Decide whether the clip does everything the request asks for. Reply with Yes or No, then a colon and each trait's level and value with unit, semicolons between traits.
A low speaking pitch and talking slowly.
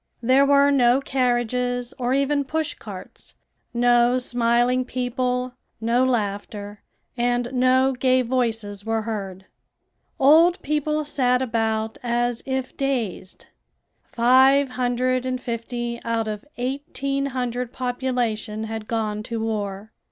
No: high, 245 Hz; slow, 115 wpm